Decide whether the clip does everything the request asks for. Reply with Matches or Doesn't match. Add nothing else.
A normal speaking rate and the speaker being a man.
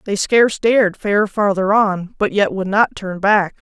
Doesn't match